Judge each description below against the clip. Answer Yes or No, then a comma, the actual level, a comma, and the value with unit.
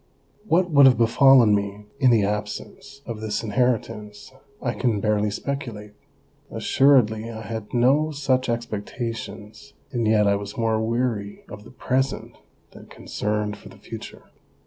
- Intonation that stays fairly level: No, average, 3.5 semitones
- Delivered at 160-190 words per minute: No, average, 145 wpm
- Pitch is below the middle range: Yes, low, 115 Hz